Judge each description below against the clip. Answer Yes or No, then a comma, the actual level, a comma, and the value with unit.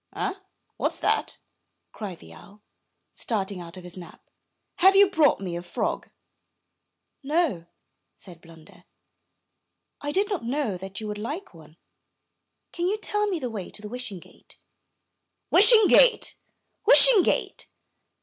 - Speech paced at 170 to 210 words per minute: No, average, 140 wpm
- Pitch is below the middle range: No, high, 220 Hz